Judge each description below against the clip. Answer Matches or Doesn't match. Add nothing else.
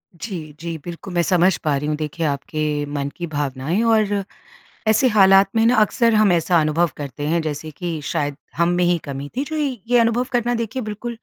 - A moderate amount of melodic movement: Doesn't match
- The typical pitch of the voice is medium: Matches